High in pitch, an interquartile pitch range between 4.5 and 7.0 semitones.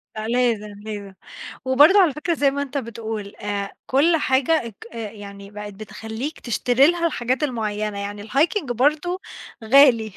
Yes: high, 235 Hz; average, 5.2 semitones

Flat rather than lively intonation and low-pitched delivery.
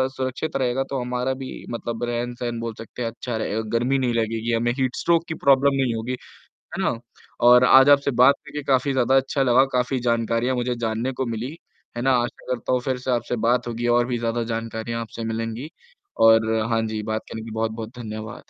Yes: narrow, 2.3 semitones; low, 120 Hz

